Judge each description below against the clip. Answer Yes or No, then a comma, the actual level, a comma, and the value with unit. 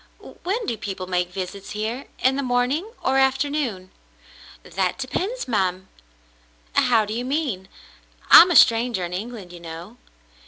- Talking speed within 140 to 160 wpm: Yes, average, 155 wpm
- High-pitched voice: Yes, high, 230 Hz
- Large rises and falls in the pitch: Yes, wide, 6.2 semitones